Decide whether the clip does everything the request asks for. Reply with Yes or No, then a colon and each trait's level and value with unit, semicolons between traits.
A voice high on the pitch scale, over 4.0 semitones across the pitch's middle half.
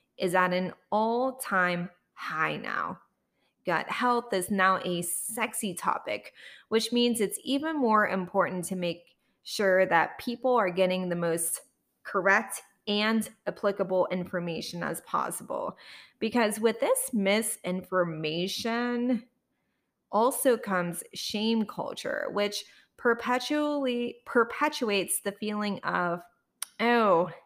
Yes: high, 205 Hz; average, 4.6 semitones